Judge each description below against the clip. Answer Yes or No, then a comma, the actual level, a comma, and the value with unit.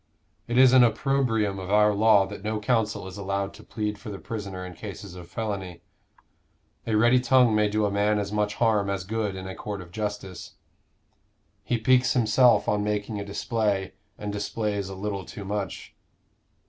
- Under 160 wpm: No, average, 185 wpm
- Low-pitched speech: Yes, low, 105 Hz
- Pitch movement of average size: No, narrow, 2.0 semitones